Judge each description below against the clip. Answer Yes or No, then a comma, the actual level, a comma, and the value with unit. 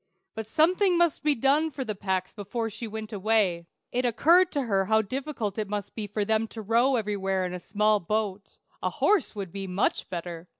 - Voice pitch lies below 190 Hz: No, high, 215 Hz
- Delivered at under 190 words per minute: No, fast, 205 wpm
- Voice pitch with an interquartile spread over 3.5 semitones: Yes, average, 4.3 semitones